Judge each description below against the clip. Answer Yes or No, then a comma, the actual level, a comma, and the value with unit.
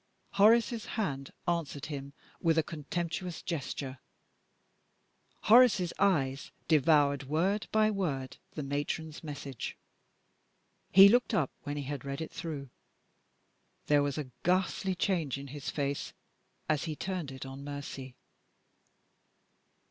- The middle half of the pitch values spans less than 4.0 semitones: No, average, 4.6 semitones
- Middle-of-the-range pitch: Yes, medium, 150 Hz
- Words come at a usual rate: No, slow, 120 wpm